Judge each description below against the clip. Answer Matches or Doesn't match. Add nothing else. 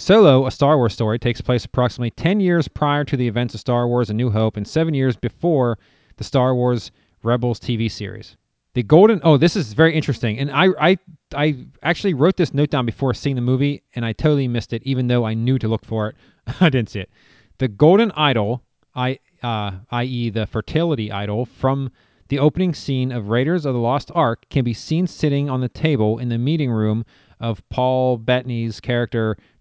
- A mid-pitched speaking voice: Doesn't match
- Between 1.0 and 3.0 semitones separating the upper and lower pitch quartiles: Doesn't match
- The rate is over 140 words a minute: Matches